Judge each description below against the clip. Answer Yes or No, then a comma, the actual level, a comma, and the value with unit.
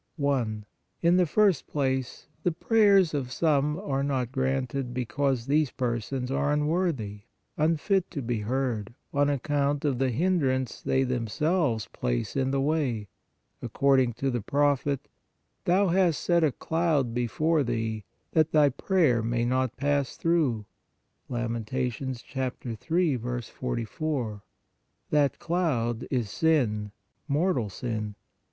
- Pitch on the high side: No, low, 135 Hz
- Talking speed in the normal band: No, slow, 130 wpm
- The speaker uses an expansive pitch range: No, average, 4.3 semitones